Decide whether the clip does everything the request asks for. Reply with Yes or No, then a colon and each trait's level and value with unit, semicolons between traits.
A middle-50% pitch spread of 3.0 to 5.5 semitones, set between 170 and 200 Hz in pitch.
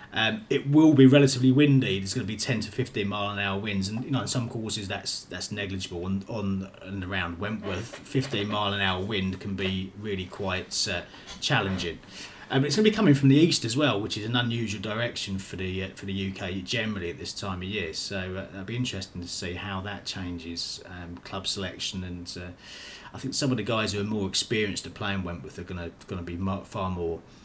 No: average, 3.7 semitones; low, 100 Hz